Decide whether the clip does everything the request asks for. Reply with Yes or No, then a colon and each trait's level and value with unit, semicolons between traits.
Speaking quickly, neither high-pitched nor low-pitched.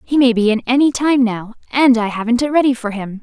No: fast, 260 wpm; high, 240 Hz